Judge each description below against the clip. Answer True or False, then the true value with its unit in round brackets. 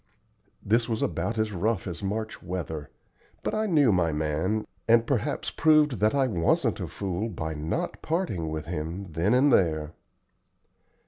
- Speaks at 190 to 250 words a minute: False (160 wpm)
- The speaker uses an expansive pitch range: True (6.1 semitones)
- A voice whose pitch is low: True (100 Hz)